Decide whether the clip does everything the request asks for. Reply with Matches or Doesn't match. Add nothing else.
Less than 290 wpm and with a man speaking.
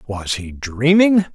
Matches